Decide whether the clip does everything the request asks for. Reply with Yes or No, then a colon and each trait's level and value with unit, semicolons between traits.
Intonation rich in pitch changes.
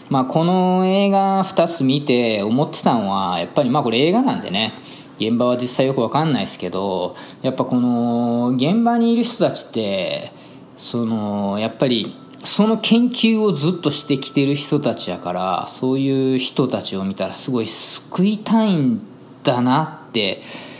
Yes: wide, 7.5 semitones